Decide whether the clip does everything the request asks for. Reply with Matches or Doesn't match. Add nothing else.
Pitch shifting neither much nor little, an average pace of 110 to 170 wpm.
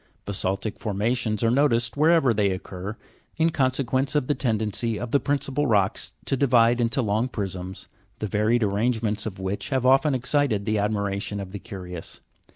Matches